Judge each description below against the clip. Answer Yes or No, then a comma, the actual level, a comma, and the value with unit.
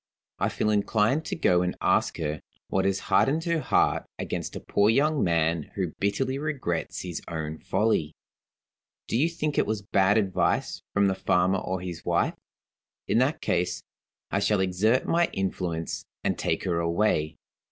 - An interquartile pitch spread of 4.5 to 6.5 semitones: Yes, average, 4.8 semitones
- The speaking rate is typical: Yes, average, 165 wpm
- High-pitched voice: No, very low, 95 Hz